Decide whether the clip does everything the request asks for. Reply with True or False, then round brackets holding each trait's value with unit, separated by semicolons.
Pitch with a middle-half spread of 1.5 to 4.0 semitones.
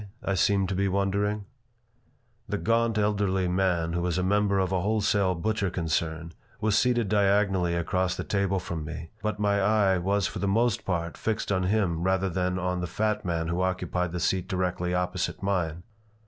True (2.4 semitones)